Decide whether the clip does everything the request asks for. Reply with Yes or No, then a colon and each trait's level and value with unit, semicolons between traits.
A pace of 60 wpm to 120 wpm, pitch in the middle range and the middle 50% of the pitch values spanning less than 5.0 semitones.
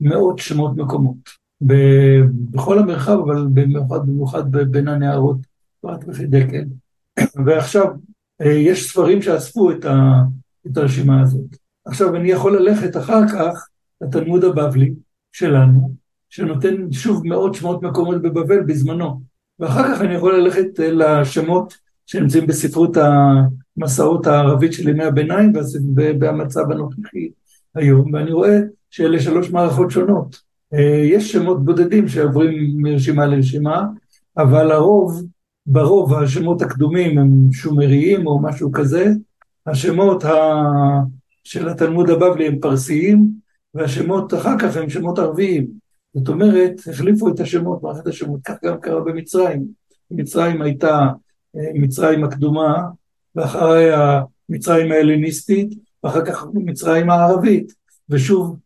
Yes: average, 115 wpm; medium, 155 Hz; average, 3.9 semitones